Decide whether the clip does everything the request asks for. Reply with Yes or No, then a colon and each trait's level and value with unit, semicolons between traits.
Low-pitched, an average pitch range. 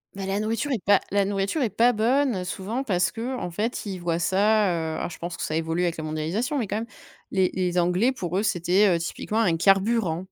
No: high, 195 Hz; average, 4.2 semitones